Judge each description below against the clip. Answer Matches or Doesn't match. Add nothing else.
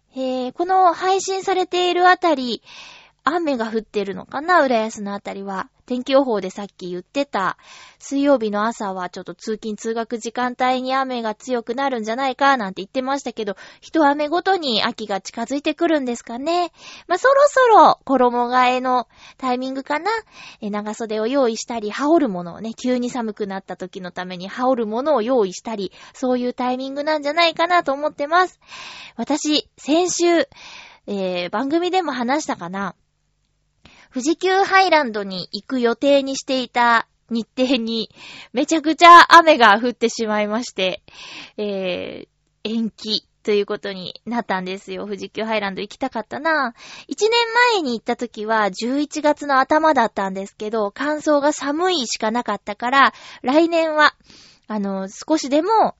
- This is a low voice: Doesn't match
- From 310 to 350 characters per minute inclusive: Matches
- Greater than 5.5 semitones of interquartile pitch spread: Matches